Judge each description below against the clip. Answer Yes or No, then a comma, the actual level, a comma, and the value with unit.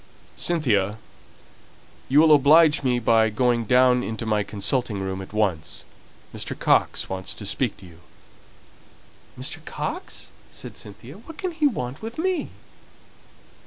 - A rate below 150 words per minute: Yes, slow, 135 wpm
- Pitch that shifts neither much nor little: No, wide, 6.7 semitones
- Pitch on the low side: Yes, low, 120 Hz